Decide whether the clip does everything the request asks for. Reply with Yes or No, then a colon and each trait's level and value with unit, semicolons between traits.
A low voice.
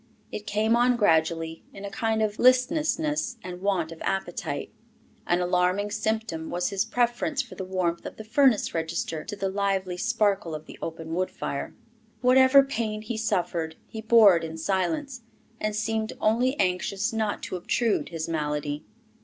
No: high, 205 Hz